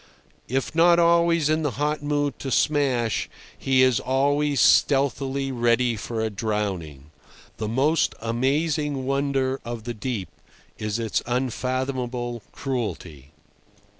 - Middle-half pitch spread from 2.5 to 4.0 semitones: Yes, average, 3.7 semitones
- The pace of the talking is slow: Yes, slow, 120 wpm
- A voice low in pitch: Yes, low, 130 Hz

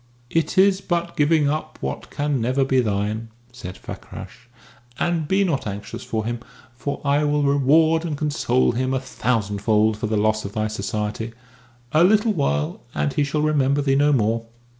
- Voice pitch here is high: No, low, 135 Hz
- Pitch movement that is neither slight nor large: No, wide, 5.9 semitones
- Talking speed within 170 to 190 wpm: Yes, average, 175 wpm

